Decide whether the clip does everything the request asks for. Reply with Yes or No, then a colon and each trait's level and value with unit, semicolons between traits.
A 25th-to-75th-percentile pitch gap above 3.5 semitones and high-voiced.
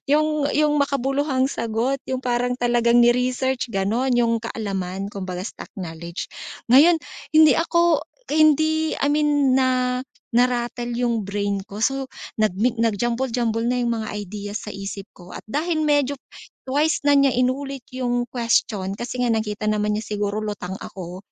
Yes: average, 4.4 semitones; high, 240 Hz